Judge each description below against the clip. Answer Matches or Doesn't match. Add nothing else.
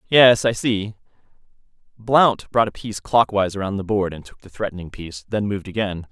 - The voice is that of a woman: Doesn't match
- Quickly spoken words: Doesn't match